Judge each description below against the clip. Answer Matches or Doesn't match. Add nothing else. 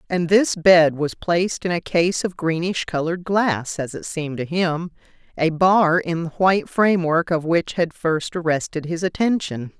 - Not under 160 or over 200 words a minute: Matches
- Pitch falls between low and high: Matches